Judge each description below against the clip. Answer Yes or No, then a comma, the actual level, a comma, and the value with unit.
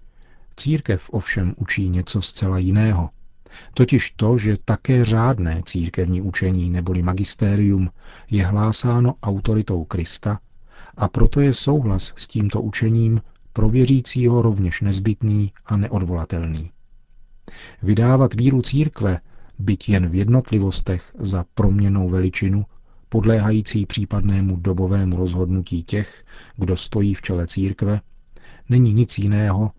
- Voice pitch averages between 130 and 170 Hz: No, low, 100 Hz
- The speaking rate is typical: No, slow, 110 wpm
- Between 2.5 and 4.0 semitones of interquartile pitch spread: Yes, average, 3.5 semitones